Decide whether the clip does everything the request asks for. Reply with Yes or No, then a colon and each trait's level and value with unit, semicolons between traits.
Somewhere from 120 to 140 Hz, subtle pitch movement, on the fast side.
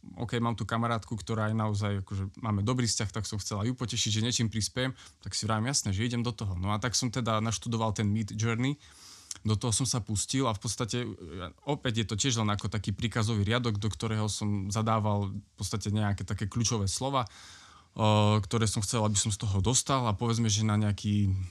No: low, 110 Hz; narrow, 2.3 semitones; fast, 210 wpm